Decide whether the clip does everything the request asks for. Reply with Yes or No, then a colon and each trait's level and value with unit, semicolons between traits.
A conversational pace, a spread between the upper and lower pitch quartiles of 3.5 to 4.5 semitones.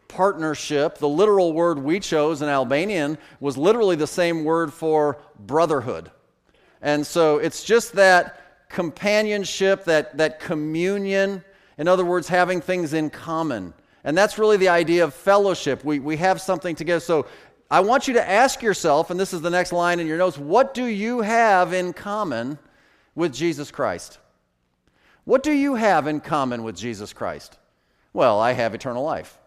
Yes: average, 165 wpm; average, 4.2 semitones